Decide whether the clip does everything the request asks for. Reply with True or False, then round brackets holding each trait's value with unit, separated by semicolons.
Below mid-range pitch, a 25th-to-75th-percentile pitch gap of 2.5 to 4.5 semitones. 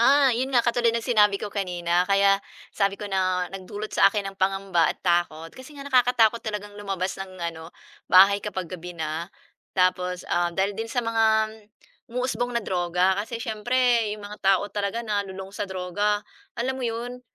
False (205 Hz; 3.8 semitones)